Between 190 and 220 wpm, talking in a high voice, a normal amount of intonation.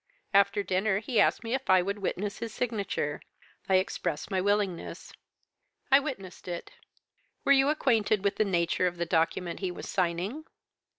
No: average, 165 wpm; high, 200 Hz; average, 3.5 semitones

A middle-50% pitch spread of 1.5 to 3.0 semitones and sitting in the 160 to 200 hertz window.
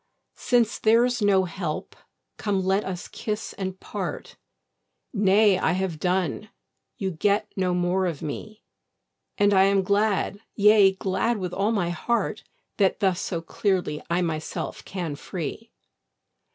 Yes: average, 2.7 semitones; high, 190 Hz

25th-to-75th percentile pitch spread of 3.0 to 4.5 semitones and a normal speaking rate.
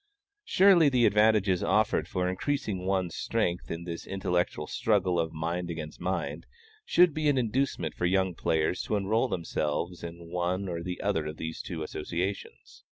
Yes: average, 3.9 semitones; average, 160 wpm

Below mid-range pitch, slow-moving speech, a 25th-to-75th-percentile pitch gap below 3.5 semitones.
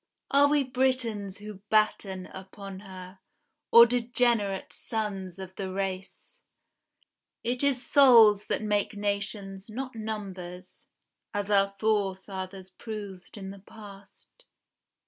No: high, 205 Hz; slow, 110 wpm; average, 2.8 semitones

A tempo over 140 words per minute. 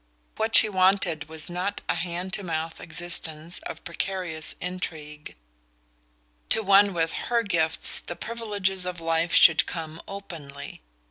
No: slow, 135 wpm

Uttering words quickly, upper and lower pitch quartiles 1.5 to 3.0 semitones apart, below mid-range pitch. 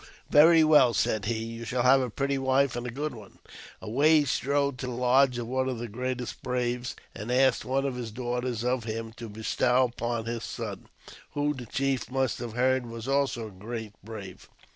Yes: fast, 210 wpm; narrow, 2.4 semitones; low, 125 Hz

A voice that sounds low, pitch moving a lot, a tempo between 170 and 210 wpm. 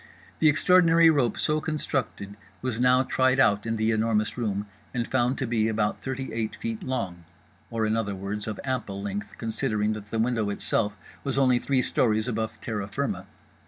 No: low, 115 Hz; average, 3.5 semitones; average, 180 wpm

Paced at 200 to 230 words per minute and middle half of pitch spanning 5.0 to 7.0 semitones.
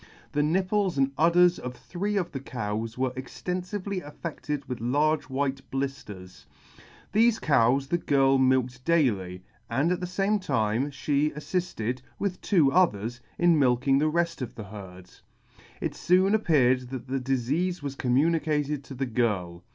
No: average, 155 wpm; wide, 5.5 semitones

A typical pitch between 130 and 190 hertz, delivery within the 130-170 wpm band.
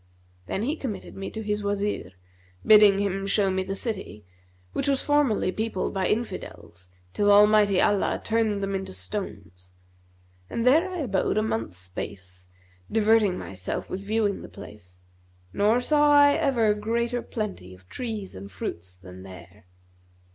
No: high, 200 Hz; average, 150 wpm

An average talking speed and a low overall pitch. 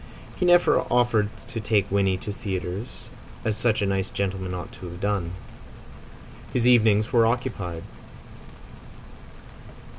No: slow, 125 wpm; low, 105 Hz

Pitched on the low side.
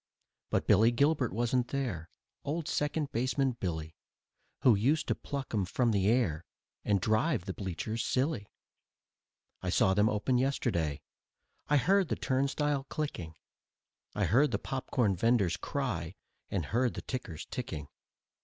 Yes: low, 120 Hz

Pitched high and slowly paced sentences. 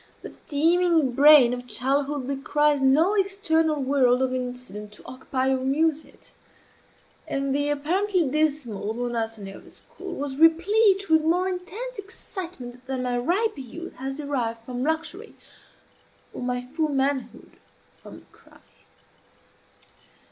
Yes: very high, 285 Hz; slow, 130 wpm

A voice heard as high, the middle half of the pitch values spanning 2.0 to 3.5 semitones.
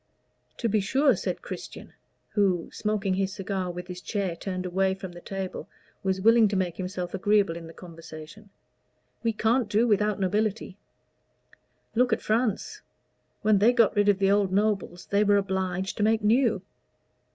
Yes: high, 200 Hz; narrow, 2.5 semitones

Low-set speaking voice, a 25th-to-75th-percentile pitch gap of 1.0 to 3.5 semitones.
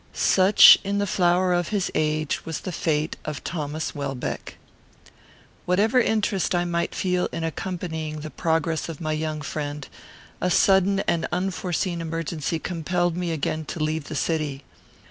No: medium, 165 Hz; average, 2.7 semitones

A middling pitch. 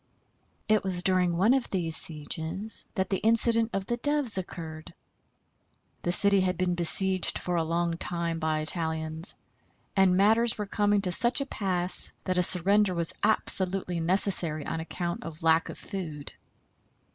Yes: medium, 180 Hz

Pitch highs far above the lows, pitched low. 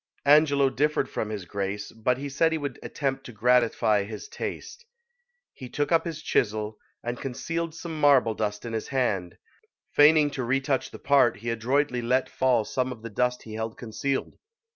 No: average, 4.3 semitones; low, 125 Hz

